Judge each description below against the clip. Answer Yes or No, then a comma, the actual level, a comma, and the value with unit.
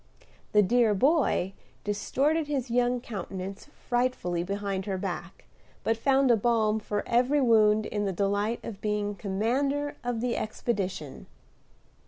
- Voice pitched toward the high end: Yes, high, 215 Hz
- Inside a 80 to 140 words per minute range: Yes, slow, 135 wpm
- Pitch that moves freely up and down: No, average, 3.7 semitones